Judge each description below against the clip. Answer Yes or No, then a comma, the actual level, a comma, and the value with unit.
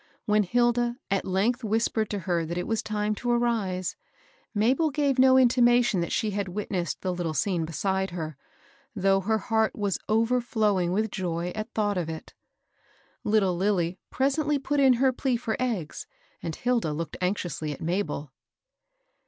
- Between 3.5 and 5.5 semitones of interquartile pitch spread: Yes, average, 4.9 semitones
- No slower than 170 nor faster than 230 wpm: No, average, 160 wpm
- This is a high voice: Yes, high, 210 Hz